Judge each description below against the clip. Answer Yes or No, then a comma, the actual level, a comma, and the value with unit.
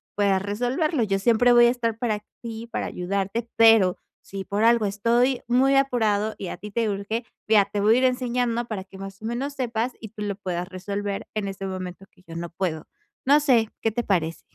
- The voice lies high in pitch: Yes, high, 215 Hz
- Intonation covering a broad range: No, average, 3.4 semitones